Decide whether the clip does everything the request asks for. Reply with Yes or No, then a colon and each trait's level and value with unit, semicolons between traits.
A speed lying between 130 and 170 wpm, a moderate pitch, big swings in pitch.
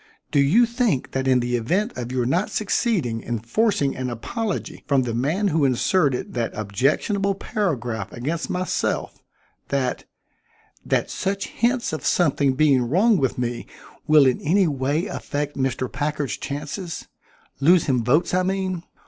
Yes: average, 150 wpm; medium, 145 Hz; wide, 6.7 semitones